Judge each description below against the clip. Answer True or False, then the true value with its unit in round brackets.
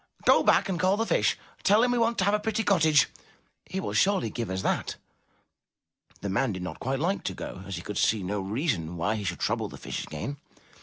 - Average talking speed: False (235 wpm)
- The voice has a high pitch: False (135 Hz)